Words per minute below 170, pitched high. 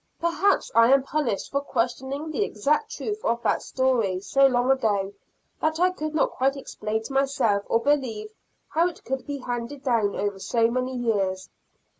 No: average, 175 wpm; very high, 260 Hz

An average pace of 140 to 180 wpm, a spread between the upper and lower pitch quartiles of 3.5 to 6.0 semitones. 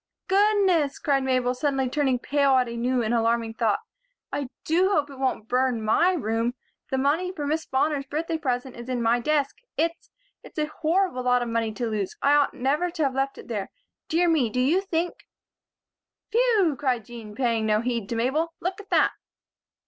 No: average, 195 wpm; average, 5.0 semitones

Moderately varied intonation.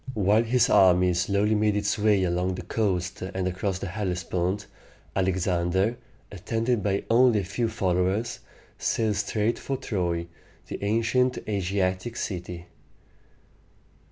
Yes: average, 3.1 semitones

